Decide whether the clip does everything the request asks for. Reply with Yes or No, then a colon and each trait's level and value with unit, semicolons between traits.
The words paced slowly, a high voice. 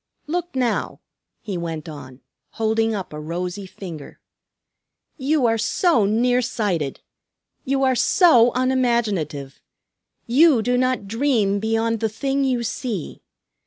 Yes: slow, 125 wpm; high, 225 Hz